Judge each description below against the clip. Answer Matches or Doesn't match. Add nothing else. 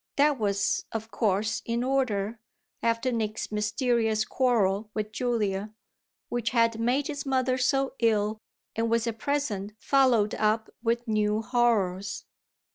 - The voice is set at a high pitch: Matches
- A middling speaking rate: Doesn't match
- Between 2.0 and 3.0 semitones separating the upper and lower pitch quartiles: Matches